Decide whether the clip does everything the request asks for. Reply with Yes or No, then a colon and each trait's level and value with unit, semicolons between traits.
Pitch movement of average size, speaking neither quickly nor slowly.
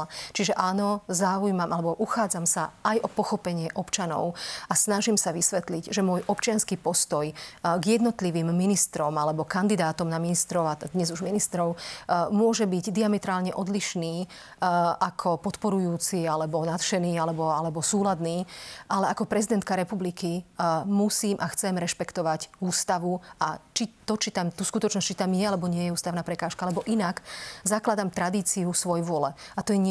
Yes: average, 3.1 semitones; average, 150 wpm